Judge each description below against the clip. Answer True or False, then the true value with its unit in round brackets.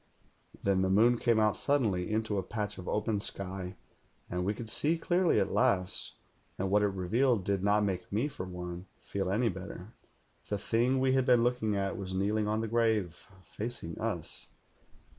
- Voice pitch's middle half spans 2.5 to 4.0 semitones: True (3.6 semitones)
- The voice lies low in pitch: True (105 Hz)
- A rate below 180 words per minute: False (185 wpm)